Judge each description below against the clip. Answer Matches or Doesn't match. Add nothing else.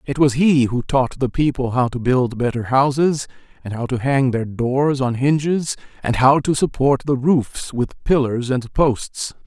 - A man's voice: Matches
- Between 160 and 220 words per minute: Matches